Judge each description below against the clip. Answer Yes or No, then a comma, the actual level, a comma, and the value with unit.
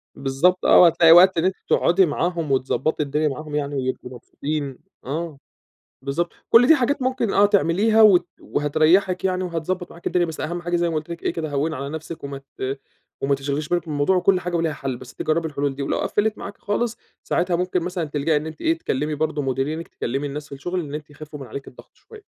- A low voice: No, medium, 160 Hz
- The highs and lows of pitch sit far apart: No, average, 3.9 semitones